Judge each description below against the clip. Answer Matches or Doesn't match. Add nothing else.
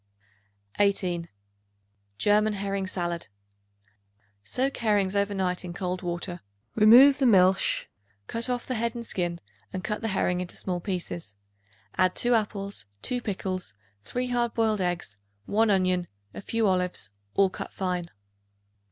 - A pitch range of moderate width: Matches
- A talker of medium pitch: Doesn't match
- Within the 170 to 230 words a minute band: Doesn't match